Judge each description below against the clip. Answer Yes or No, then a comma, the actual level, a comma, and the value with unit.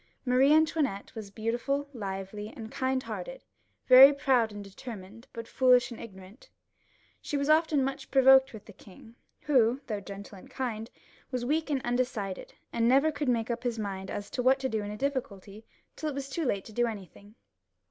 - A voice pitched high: Yes, high, 240 Hz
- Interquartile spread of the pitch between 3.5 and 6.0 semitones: Yes, average, 4.3 semitones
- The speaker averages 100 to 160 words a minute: No, average, 190 wpm